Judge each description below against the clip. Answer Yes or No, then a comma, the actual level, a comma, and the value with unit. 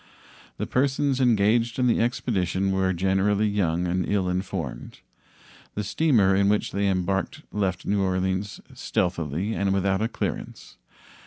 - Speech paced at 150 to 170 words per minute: No, average, 140 wpm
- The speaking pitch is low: Yes, low, 100 Hz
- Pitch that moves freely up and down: No, narrow, 2.4 semitones